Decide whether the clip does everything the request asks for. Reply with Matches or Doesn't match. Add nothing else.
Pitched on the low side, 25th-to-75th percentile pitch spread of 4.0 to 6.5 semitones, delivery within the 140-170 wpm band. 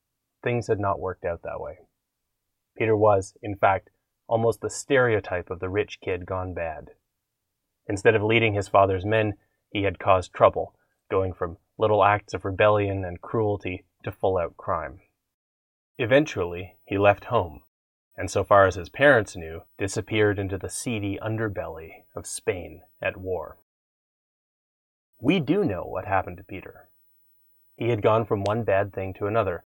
Doesn't match